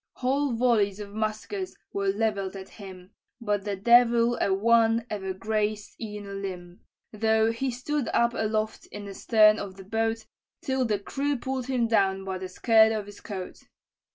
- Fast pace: No, average, 175 wpm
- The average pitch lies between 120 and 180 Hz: No, high, 215 Hz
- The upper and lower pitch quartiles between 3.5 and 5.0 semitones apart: No, average, 2.8 semitones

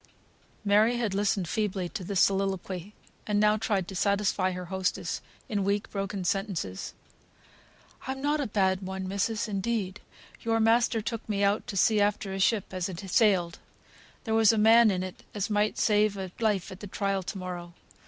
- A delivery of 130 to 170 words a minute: No, average, 180 wpm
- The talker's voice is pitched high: Yes, high, 200 Hz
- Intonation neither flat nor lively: No, narrow, 2.3 semitones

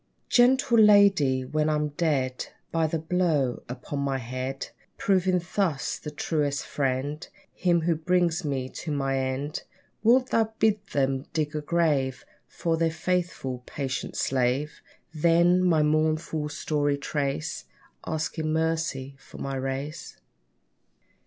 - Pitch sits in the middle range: Yes, medium, 150 Hz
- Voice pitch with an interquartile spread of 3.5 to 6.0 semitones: Yes, average, 3.9 semitones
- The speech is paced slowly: Yes, slow, 125 wpm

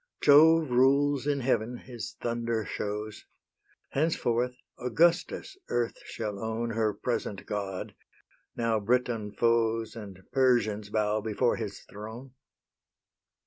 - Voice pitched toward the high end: No, low, 115 Hz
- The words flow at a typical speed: No, slow, 105 wpm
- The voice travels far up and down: No, average, 2.9 semitones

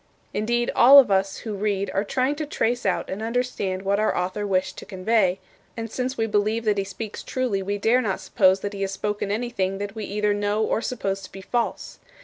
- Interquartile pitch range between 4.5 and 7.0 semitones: No, average, 2.8 semitones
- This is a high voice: Yes, high, 205 Hz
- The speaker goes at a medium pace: No, fast, 220 wpm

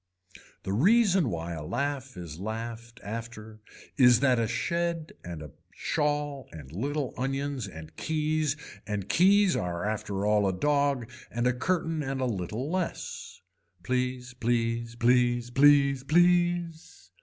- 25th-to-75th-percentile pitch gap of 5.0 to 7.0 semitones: Yes, average, 5.3 semitones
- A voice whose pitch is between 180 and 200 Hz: No, low, 125 Hz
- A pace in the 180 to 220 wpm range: No, slow, 135 wpm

